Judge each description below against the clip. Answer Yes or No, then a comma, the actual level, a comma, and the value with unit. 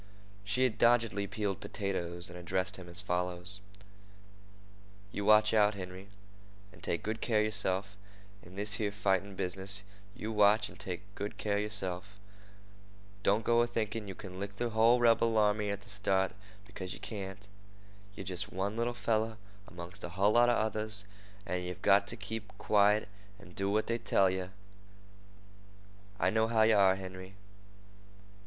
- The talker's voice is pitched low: Yes, low, 100 Hz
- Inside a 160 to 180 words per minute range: Yes, average, 165 wpm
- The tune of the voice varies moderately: No, narrow, 2.2 semitones